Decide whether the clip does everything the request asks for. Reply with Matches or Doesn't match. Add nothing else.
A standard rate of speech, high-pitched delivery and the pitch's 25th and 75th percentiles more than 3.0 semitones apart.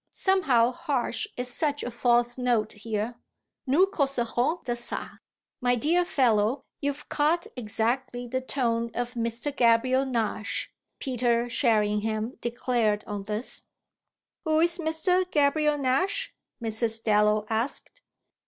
Doesn't match